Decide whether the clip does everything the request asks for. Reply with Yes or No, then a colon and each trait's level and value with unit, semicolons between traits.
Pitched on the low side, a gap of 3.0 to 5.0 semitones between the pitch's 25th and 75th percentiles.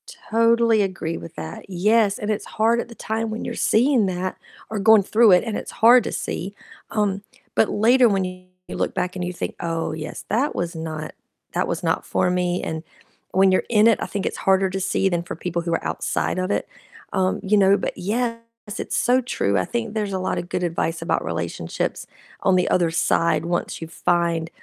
No: high, 190 Hz; average, 4.0 semitones